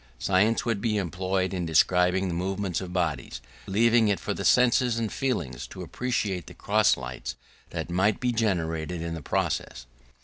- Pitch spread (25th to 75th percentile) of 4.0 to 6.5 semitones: Yes, average, 4.5 semitones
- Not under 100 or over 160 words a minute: No, average, 170 wpm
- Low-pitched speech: Yes, very low, 95 Hz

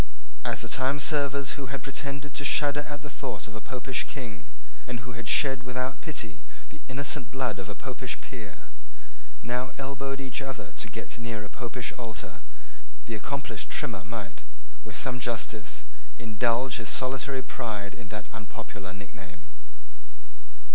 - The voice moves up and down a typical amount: Yes, average, 3.9 semitones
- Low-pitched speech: Yes, low, 125 Hz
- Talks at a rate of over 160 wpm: No, average, 155 wpm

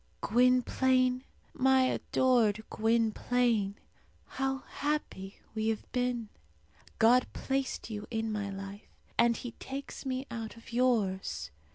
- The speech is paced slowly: Yes, slow, 110 wpm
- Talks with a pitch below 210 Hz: No, high, 235 Hz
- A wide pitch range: No, average, 2.9 semitones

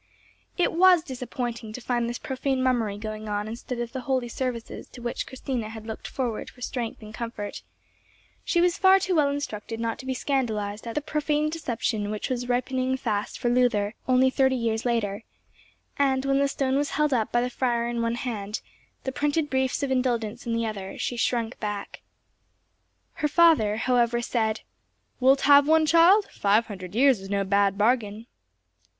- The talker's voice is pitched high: Yes, high, 245 Hz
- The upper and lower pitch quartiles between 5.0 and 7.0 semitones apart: No, average, 3.4 semitones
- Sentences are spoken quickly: No, average, 180 wpm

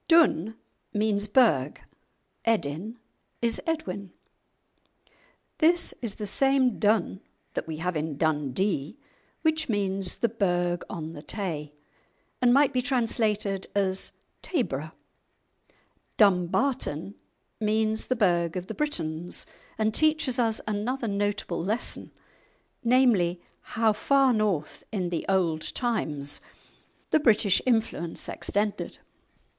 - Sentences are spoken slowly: Yes, slow, 110 wpm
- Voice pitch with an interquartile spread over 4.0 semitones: Yes, average, 5.3 semitones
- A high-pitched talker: Yes, high, 205 Hz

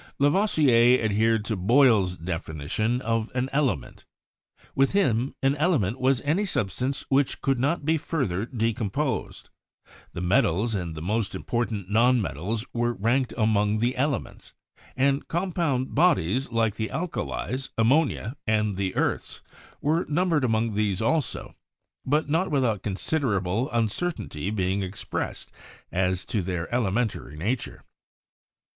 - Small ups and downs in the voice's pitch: No, average, 5.3 semitones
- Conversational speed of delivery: No, slow, 130 wpm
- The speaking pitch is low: Yes, low, 115 Hz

